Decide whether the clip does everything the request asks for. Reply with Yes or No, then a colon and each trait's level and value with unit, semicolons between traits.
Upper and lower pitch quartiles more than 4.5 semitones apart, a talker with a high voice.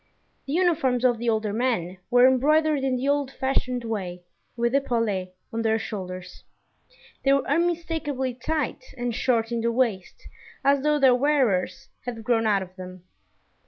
No: average, 3.9 semitones; high, 245 Hz